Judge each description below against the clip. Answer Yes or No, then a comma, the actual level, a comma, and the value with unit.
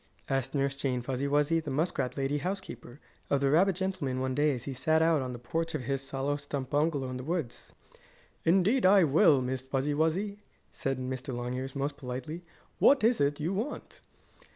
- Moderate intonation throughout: Yes, average, 3.8 semitones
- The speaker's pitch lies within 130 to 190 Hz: Yes, medium, 140 Hz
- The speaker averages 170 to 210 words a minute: Yes, average, 190 wpm